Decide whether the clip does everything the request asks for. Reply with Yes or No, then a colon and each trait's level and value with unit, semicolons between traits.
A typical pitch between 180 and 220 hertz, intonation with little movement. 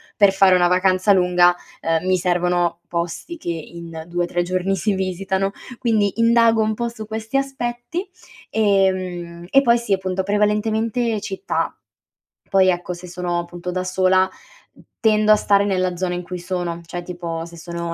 No: medium, 185 Hz; average, 3.2 semitones